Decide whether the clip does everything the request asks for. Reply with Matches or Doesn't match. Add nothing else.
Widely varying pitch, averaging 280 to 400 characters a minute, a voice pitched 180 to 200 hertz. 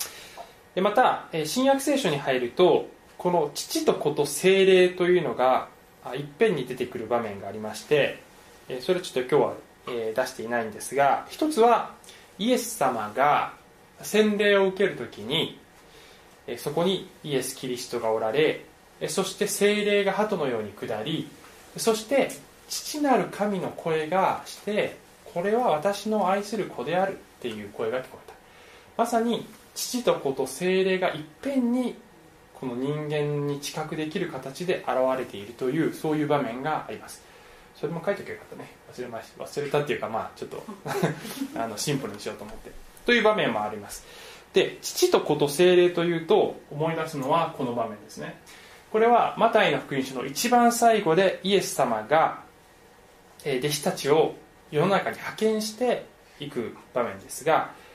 Matches